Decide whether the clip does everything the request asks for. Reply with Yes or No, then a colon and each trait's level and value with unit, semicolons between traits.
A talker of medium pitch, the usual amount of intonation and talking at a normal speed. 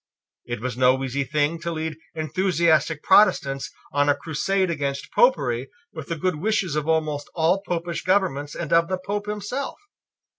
Yes: medium, 160 Hz; average, 4.4 semitones; average, 160 wpm